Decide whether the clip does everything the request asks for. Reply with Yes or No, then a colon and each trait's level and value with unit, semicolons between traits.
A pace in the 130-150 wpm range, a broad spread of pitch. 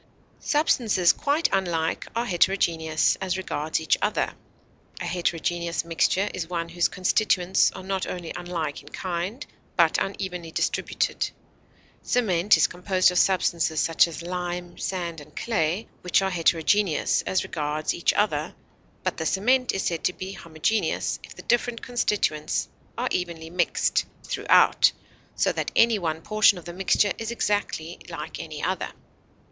No: average, 145 wpm; average, 2.8 semitones